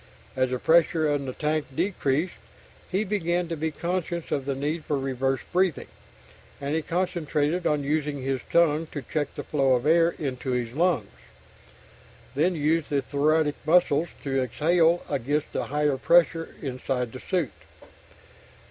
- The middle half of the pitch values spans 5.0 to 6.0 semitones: No, average, 3.7 semitones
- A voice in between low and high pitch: Yes, medium, 150 Hz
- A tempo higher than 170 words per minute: No, average, 155 wpm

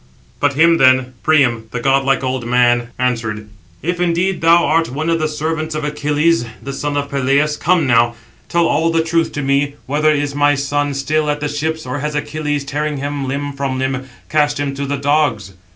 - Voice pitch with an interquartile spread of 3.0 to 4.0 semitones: No, narrow, 2.4 semitones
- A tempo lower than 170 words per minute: No, average, 200 wpm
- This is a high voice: No, medium, 145 Hz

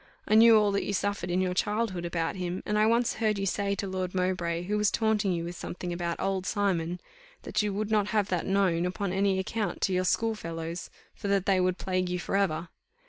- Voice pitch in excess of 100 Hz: Yes, high, 190 Hz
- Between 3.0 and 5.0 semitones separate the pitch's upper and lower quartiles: No, narrow, 2.5 semitones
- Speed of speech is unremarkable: No, fast, 235 wpm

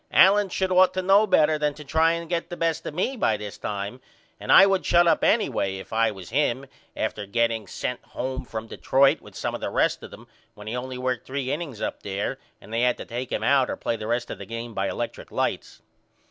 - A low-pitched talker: Yes, low, 130 Hz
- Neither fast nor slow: No, fast, 245 wpm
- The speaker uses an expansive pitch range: Yes, wide, 6.7 semitones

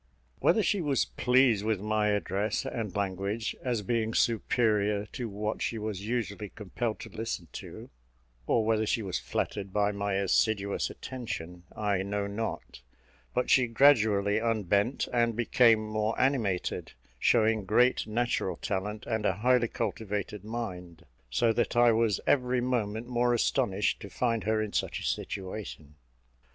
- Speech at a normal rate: Yes, average, 145 wpm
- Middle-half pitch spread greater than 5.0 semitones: No, narrow, 2.6 semitones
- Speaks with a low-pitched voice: Yes, low, 110 Hz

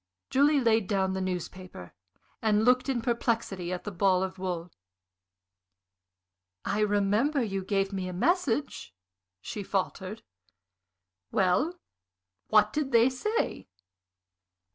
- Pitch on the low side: No, high, 205 Hz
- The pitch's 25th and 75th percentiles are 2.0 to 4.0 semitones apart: No, average, 4.8 semitones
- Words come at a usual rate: No, slow, 115 wpm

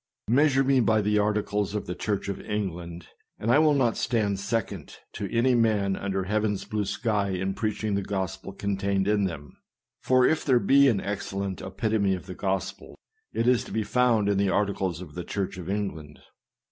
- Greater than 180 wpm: Yes, average, 190 wpm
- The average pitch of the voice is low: Yes, low, 100 Hz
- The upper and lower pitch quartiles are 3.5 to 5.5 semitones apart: No, narrow, 2.5 semitones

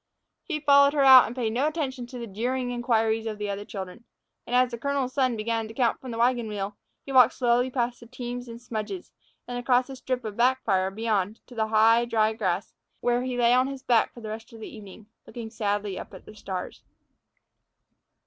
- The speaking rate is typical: No, fast, 215 wpm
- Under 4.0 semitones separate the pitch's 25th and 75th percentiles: Yes, narrow, 2.6 semitones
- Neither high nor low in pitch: No, high, 235 Hz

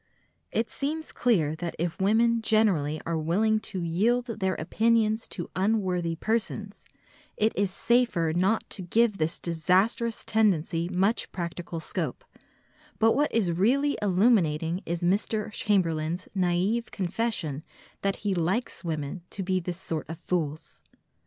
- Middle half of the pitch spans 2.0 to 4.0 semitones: No, average, 4.7 semitones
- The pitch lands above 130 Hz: Yes, high, 190 Hz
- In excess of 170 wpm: No, slow, 135 wpm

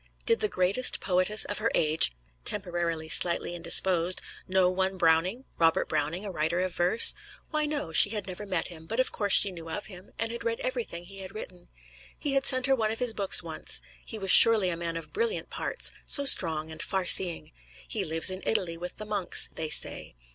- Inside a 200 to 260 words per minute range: Yes, fast, 205 wpm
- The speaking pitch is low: No, medium, 185 Hz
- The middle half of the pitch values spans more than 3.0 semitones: Yes, average, 4.7 semitones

